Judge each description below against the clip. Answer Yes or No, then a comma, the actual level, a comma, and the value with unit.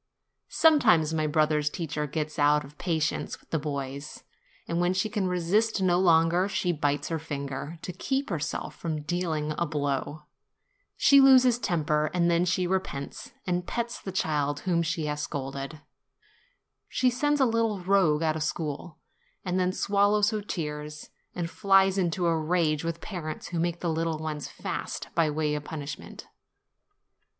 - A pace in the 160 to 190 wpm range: Yes, average, 165 wpm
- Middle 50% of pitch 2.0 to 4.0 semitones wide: Yes, average, 3.6 semitones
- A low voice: No, medium, 165 Hz